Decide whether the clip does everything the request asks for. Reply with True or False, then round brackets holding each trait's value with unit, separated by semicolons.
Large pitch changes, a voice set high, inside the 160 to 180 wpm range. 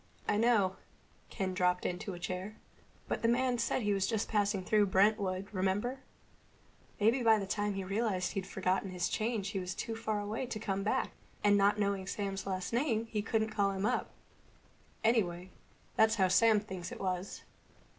False (2.7 semitones; 205 Hz; 175 wpm)